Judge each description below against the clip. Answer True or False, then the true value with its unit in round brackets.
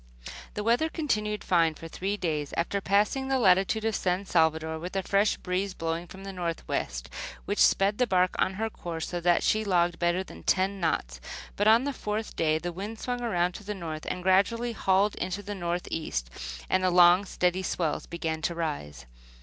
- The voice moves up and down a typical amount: True (3.5 semitones)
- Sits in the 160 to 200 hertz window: True (185 Hz)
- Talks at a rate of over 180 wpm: True (200 wpm)